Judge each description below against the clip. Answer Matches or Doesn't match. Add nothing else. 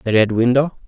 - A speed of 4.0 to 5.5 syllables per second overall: Doesn't match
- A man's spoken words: Matches